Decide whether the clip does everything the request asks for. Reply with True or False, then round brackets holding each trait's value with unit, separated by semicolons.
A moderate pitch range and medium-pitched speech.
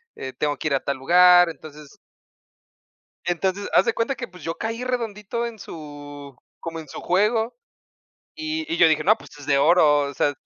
False (7.2 semitones; 175 Hz)